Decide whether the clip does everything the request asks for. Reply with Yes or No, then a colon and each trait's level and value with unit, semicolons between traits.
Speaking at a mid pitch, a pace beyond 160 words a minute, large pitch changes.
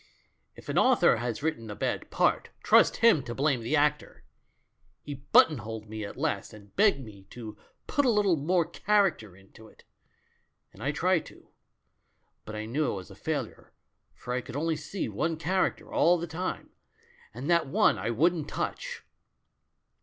Yes: medium, 145 Hz; average, 180 wpm; wide, 7.2 semitones